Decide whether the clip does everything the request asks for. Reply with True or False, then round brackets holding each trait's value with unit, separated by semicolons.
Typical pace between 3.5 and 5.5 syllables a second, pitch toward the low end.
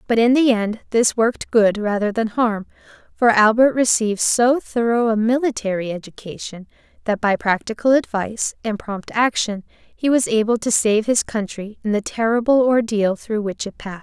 False (5.0 syllables/s; 220 Hz)